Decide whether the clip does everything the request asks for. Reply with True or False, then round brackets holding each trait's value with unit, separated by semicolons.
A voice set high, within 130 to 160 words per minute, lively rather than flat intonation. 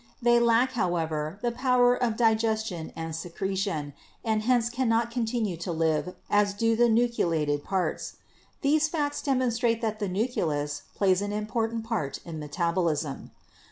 True (215 Hz; 140 wpm; 5.9 semitones)